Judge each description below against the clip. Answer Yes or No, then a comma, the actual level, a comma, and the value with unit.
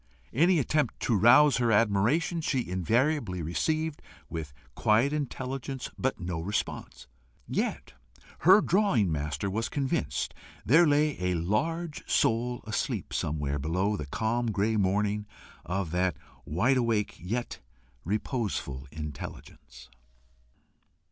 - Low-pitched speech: Yes, low, 110 Hz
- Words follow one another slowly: Yes, slow, 115 wpm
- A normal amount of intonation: No, wide, 7.1 semitones